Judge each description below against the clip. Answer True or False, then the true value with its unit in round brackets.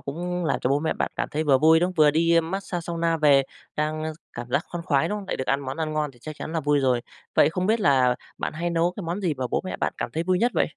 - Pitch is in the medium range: True (160 Hz)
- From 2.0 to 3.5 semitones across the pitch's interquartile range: True (3.2 semitones)